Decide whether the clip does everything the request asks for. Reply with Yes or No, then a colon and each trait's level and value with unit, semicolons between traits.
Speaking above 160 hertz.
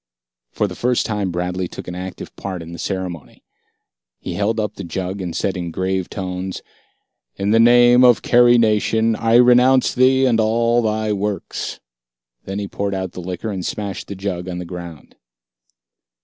No: low, 100 Hz